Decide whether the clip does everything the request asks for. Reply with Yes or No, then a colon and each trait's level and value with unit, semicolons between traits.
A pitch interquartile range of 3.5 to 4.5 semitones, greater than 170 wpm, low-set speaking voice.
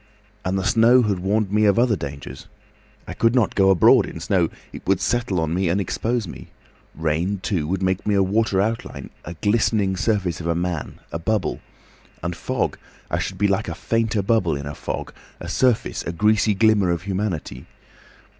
Yes: average, 3.9 semitones; average, 185 wpm; very low, 95 Hz